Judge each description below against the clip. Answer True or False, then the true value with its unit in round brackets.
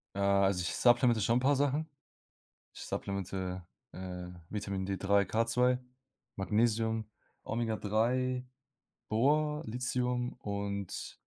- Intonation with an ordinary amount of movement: True (4.1 semitones)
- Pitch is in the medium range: False (110 Hz)